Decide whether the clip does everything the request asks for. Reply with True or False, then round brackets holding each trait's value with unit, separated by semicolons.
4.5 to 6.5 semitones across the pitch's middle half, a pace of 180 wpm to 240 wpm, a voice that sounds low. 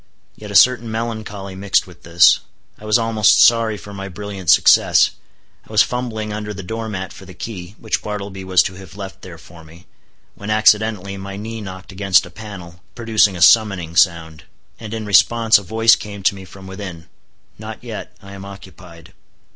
False (2.7 semitones; 185 wpm; 100 Hz)